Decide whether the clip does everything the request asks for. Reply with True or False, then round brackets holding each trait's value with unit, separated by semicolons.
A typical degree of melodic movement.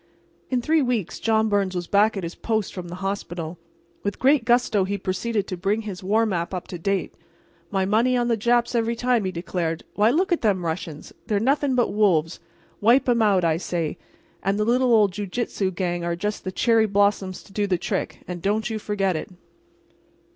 True (3.9 semitones)